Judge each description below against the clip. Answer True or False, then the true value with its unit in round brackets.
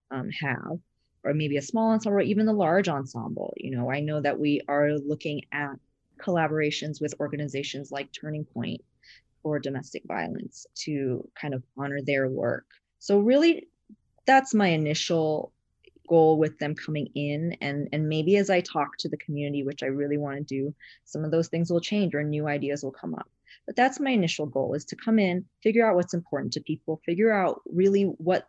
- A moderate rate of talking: True (190 wpm)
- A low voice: False (155 Hz)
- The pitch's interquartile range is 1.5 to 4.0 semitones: False (4.7 semitones)